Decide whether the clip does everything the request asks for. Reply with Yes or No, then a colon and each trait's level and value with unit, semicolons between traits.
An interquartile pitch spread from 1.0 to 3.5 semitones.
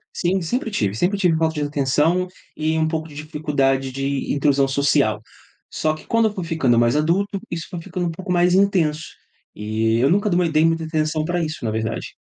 No: average, 4.1 semitones